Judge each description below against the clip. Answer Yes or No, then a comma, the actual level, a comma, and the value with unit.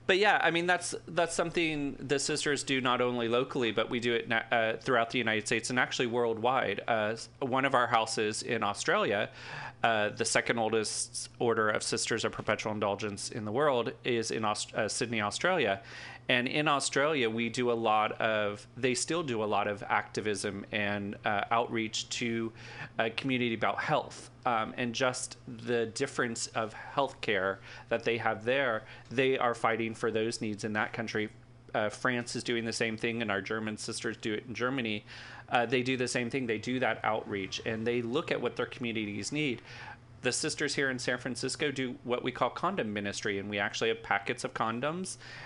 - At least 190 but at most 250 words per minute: Yes, average, 195 wpm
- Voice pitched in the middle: No, low, 120 Hz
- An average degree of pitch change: No, narrow, 2.3 semitones